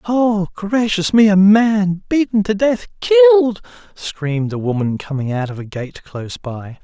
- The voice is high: No, medium, 180 Hz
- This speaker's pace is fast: No, average, 160 wpm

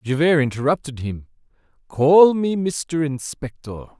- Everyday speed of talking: No, slow, 105 wpm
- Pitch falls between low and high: Yes, medium, 145 Hz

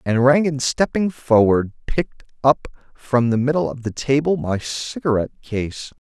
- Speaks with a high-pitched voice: No, low, 130 Hz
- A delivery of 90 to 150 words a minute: Yes, average, 140 wpm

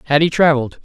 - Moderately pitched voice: Yes, medium, 150 Hz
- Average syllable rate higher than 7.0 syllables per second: Yes, 7.9 syllables/s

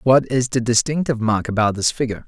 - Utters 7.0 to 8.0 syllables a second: No, 6.5 syllables/s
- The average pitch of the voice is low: Yes, low, 120 Hz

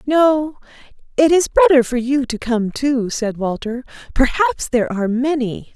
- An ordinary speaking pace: Yes, average, 155 wpm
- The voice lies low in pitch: No, very high, 265 Hz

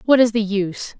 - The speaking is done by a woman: Yes, female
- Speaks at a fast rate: Yes, fast, 240 wpm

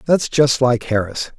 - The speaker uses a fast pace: No, average, 175 wpm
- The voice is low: Yes, low, 130 Hz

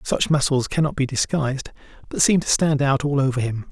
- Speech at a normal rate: No, fast, 225 wpm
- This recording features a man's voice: Yes, male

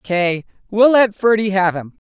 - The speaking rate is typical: Yes, average, 175 wpm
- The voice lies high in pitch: Yes, high, 200 Hz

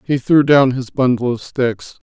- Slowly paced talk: No, fast, 205 wpm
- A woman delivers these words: No, male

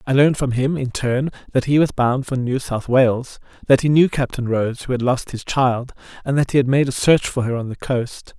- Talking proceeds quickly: Yes, fast, 260 wpm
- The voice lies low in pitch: Yes, low, 130 Hz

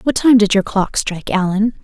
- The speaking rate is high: Yes, fast, 230 wpm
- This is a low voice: No, high, 210 Hz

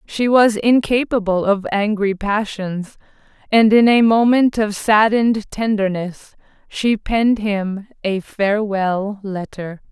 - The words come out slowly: Yes, slow, 115 wpm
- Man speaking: No, female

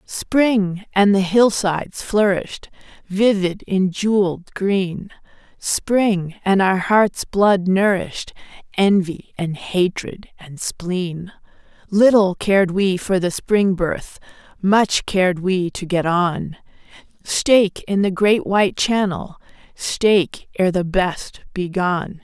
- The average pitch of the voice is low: No, high, 190 Hz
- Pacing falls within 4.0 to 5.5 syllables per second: No, 3.4 syllables/s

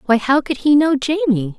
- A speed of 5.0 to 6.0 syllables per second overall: No, 6.6 syllables/s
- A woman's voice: Yes, female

